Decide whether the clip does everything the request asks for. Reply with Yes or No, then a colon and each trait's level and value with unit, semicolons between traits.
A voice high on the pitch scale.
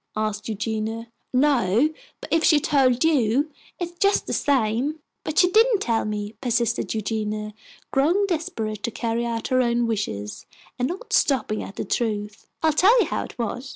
Yes: high, 235 Hz